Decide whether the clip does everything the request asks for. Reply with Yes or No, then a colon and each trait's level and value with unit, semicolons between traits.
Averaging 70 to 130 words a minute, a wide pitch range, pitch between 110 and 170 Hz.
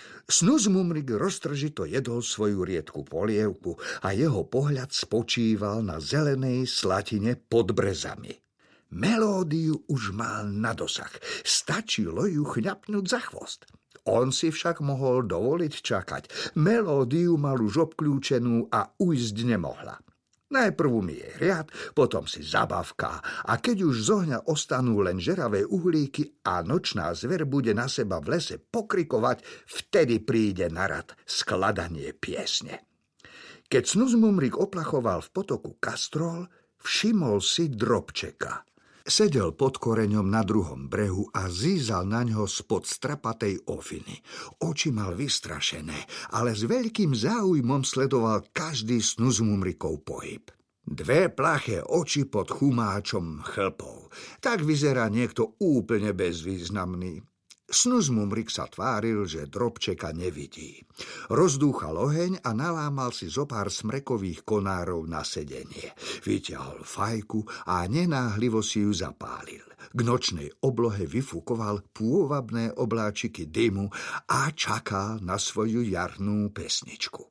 Yes: average, 120 wpm; wide, 6.3 semitones; low, 120 Hz